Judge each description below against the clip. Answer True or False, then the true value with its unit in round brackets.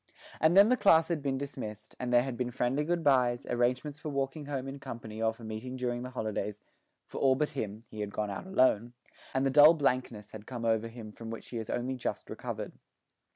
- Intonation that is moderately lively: True (3.7 semitones)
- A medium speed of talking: False (225 wpm)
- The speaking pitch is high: False (125 Hz)